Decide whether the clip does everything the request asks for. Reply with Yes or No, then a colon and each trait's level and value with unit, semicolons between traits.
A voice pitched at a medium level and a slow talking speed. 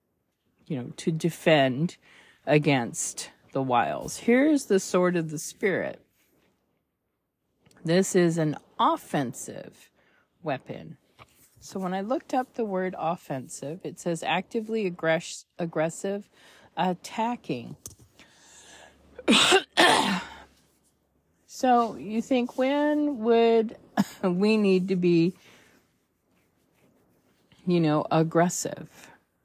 Yes: medium, 180 Hz; slow, 90 wpm